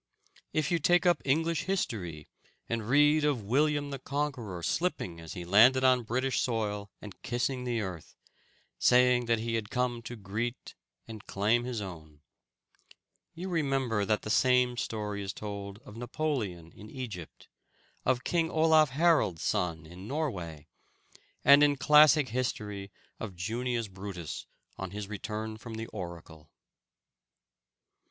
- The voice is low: Yes, low, 115 Hz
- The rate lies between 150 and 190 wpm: No, average, 140 wpm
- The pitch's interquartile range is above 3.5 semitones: Yes, average, 5.3 semitones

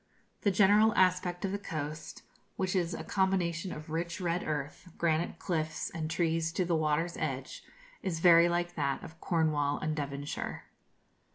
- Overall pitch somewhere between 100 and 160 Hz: No, medium, 170 Hz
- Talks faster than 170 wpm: No, average, 160 wpm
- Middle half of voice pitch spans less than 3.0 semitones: Yes, narrow, 2.6 semitones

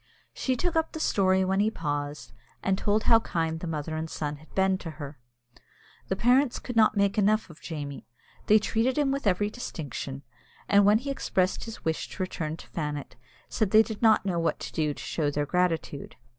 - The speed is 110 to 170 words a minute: No, fast, 205 wpm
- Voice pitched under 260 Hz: Yes, high, 190 Hz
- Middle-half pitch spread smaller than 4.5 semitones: No, wide, 5.6 semitones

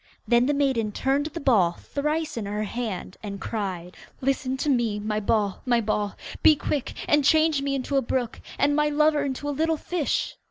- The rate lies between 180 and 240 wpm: Yes, average, 195 wpm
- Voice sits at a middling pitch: No, very high, 265 Hz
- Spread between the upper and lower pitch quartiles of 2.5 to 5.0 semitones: No, wide, 5.4 semitones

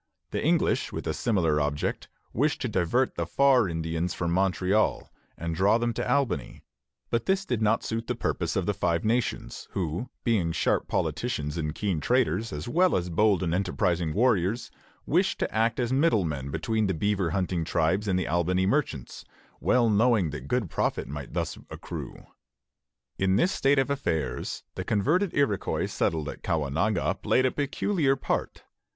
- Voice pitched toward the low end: Yes, low, 100 Hz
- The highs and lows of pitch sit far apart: Yes, wide, 6.5 semitones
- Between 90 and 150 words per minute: No, average, 170 wpm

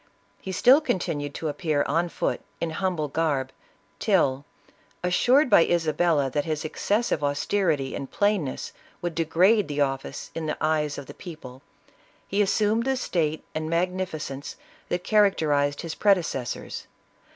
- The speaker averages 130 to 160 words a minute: Yes, average, 140 wpm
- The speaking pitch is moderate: Yes, medium, 160 Hz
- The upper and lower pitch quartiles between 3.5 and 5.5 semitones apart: Yes, average, 4.5 semitones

